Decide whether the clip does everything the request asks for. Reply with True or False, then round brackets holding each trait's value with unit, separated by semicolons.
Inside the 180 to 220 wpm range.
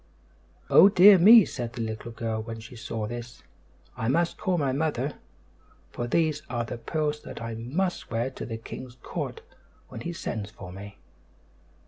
False (170 wpm)